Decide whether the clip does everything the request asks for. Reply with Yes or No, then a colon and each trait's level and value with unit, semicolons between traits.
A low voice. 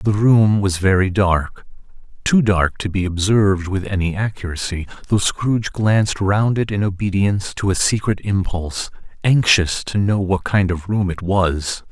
Yes: low, 100 Hz